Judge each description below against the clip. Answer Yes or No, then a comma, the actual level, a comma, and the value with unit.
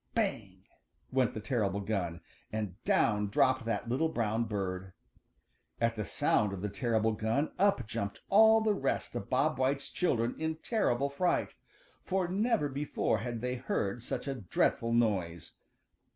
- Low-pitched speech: Yes, low, 115 Hz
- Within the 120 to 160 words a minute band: Yes, average, 150 wpm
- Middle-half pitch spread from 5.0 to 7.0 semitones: Yes, average, 5.3 semitones